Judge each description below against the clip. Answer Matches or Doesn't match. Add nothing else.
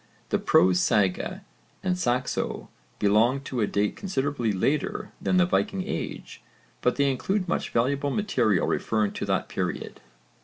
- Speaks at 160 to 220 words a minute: Doesn't match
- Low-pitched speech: Matches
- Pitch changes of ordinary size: Doesn't match